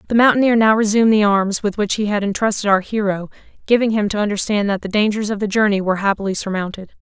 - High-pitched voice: Yes, high, 205 Hz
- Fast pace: Yes, fast, 220 wpm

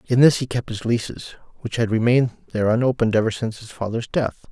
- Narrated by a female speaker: No, male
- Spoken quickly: Yes, fast, 215 wpm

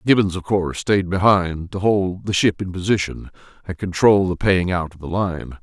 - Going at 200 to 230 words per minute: Yes, fast, 205 wpm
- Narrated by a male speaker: Yes, male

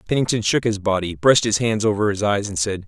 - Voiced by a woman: No, male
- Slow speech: No, fast, 250 wpm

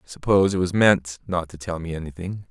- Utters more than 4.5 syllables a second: Yes, 6.0 syllables/s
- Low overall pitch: Yes, very low, 90 Hz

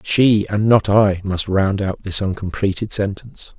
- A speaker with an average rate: Yes, average, 170 wpm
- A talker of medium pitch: No, low, 100 Hz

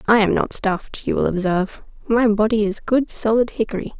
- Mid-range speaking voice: No, high, 215 Hz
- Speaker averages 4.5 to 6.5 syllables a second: Yes, 5.7 syllables/s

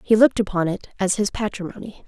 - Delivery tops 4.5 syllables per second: Yes, 6.5 syllables/s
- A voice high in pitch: Yes, high, 205 Hz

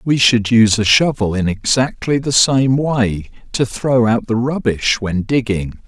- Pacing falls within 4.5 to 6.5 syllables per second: No, 4.2 syllables/s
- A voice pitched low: Yes, low, 120 Hz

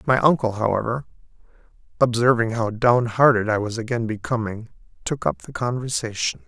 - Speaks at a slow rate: Yes, slow, 130 wpm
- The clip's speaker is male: Yes, male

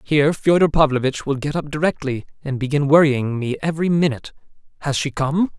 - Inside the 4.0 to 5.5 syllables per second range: No, 6.0 syllables/s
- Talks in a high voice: No, medium, 145 Hz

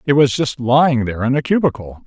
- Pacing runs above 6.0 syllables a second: Yes, 6.3 syllables/s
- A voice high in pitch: No, low, 130 Hz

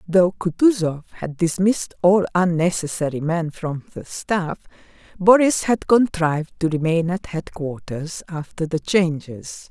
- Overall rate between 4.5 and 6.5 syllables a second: No, 4.2 syllables/s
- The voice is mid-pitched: Yes, medium, 175 Hz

